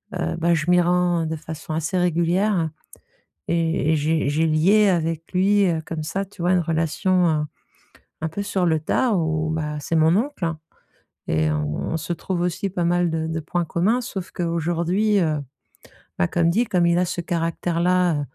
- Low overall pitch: No, medium, 170 Hz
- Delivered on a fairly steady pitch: Yes, narrow, 2.2 semitones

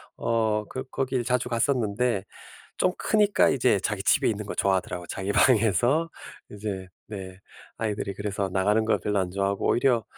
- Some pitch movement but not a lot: Yes, average, 3.9 semitones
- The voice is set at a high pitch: No, low, 105 Hz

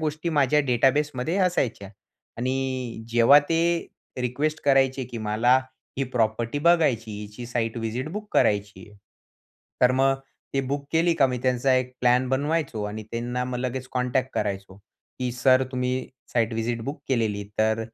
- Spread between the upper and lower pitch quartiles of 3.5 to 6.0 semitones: No, average, 3.1 semitones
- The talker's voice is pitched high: No, low, 125 Hz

